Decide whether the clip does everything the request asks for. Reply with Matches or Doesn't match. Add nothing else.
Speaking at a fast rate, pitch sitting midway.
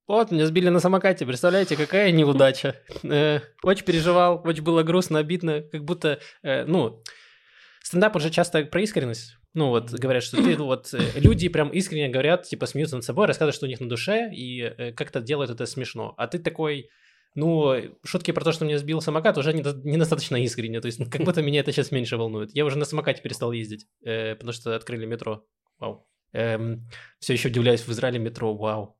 Matches